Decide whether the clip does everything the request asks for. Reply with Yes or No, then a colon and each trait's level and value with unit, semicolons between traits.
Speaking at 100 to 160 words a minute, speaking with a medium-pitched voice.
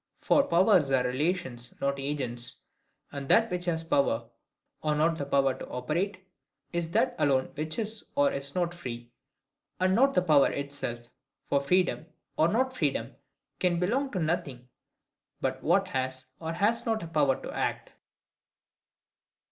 Yes: average, 155 wpm; medium, 160 Hz